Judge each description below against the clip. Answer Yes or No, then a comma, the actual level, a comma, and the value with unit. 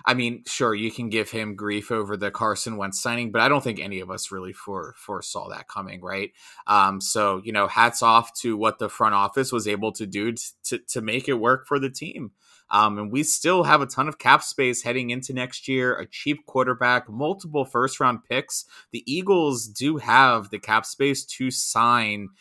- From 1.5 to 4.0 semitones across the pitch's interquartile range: Yes, average, 3.6 semitones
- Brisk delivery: Yes, fast, 215 wpm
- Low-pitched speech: Yes, low, 120 Hz